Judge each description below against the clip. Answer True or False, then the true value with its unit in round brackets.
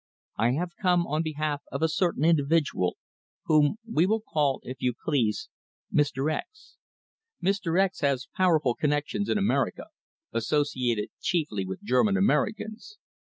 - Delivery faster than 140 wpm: False (135 wpm)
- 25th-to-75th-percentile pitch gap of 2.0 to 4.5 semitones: False (5.2 semitones)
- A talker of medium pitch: True (155 Hz)